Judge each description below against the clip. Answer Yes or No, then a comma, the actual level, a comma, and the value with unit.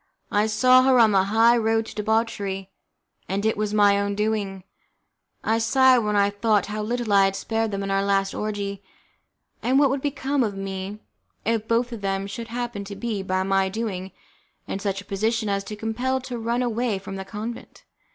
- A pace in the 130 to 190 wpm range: No, average, 200 wpm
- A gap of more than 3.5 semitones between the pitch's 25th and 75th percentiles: No, average, 2.8 semitones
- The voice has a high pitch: Yes, high, 215 Hz